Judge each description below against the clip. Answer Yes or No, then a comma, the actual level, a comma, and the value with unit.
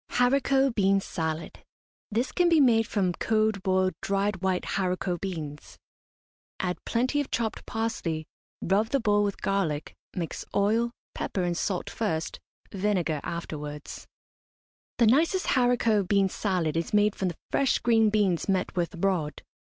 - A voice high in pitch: Yes, high, 195 Hz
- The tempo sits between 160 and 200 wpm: No, average, 145 wpm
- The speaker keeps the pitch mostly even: No, average, 4.3 semitones